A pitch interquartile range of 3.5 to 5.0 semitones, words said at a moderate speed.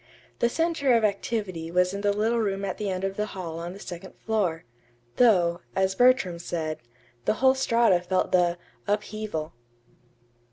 Yes: average, 4.0 semitones; average, 165 wpm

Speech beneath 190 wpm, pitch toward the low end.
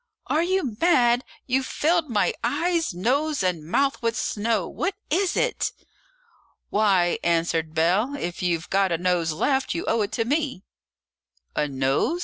No: average, 150 wpm; high, 225 Hz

